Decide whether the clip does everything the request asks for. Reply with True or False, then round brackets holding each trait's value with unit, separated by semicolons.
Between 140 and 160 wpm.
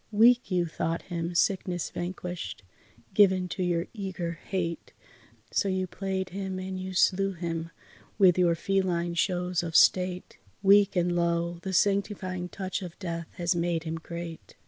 True (150 wpm)